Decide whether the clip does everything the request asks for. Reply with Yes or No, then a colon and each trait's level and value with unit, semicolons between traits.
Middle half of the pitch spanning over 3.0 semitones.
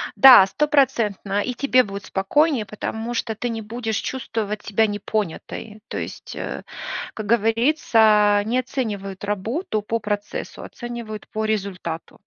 No: average, 2.7 semitones